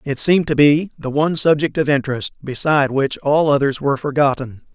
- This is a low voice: No, medium, 145 Hz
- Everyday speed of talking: Yes, average, 190 wpm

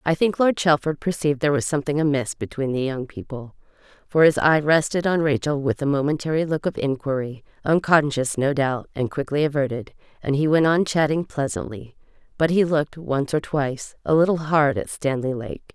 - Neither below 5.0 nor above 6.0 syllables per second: Yes, 5.5 syllables/s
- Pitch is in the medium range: Yes, medium, 145 Hz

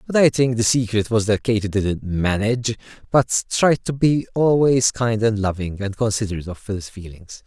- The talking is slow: No, average, 185 wpm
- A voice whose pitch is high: No, low, 110 Hz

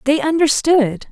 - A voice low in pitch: No, very high, 280 Hz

